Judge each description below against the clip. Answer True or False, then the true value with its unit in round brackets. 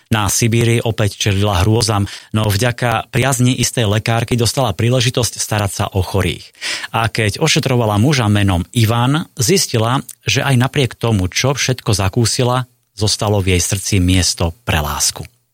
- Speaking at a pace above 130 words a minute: True (145 wpm)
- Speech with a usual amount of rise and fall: True (3.4 semitones)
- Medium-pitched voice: False (115 Hz)